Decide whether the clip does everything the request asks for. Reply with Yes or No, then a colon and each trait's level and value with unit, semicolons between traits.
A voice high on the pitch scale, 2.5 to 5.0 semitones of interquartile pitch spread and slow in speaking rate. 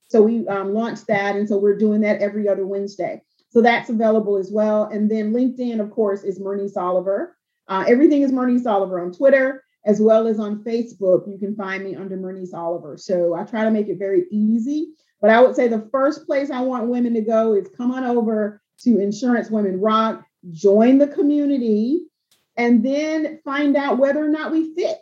No: high, 220 Hz; average, 4.3 semitones; fast, 205 wpm